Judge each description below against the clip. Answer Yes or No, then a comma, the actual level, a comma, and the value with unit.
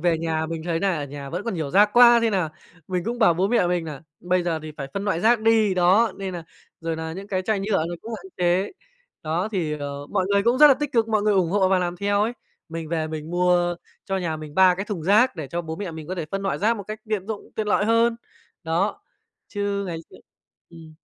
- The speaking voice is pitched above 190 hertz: No, medium, 185 Hz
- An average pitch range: Yes, average, 4.1 semitones